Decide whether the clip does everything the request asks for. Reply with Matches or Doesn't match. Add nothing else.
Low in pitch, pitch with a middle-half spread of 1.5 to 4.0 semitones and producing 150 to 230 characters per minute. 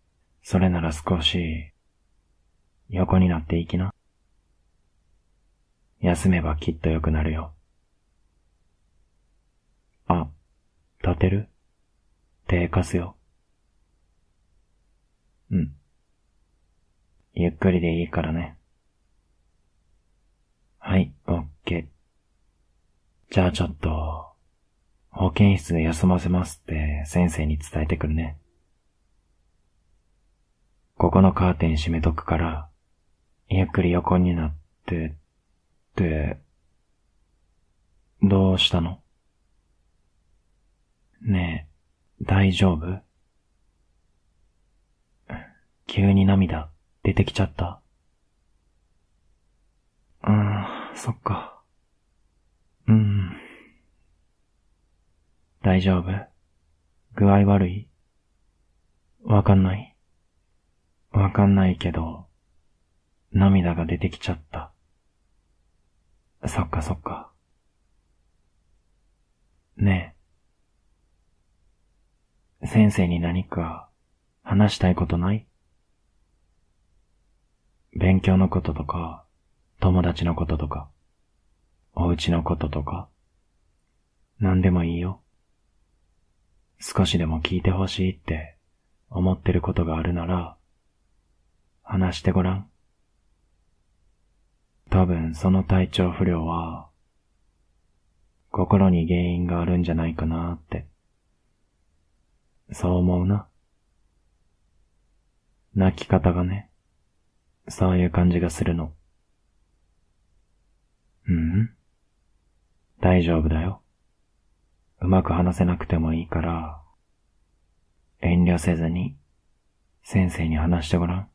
Matches